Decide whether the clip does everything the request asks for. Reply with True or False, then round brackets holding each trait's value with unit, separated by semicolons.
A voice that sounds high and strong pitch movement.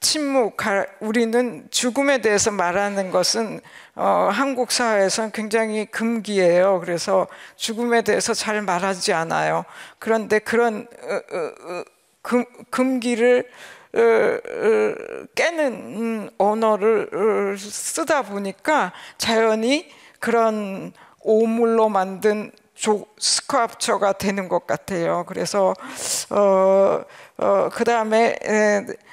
False (225 Hz; 3.6 semitones)